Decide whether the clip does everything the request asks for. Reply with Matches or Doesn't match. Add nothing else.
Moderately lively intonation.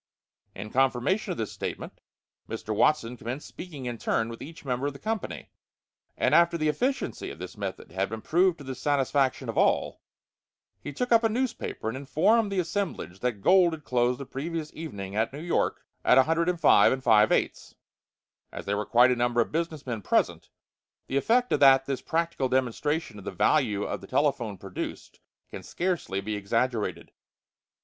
Doesn't match